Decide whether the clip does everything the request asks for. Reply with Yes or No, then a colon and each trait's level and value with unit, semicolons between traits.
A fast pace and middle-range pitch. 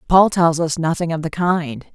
Yes: fast, 215 wpm; medium, 165 Hz